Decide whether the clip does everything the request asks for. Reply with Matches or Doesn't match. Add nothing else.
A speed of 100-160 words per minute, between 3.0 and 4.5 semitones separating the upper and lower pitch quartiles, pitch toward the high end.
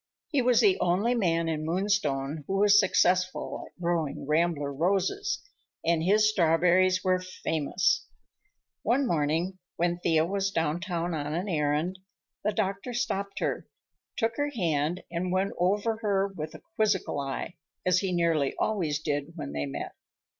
Doesn't match